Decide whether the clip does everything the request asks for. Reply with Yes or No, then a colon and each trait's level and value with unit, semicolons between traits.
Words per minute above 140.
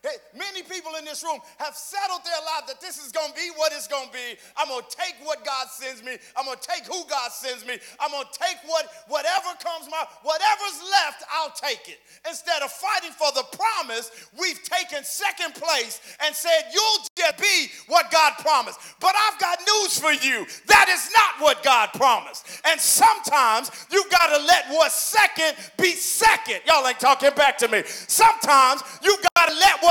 Yes: average, 195 wpm